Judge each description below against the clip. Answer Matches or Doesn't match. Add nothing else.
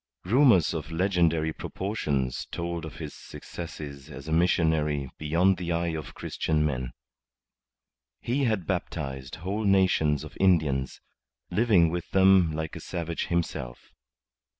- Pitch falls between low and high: Doesn't match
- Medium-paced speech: Doesn't match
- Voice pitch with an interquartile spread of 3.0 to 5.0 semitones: Matches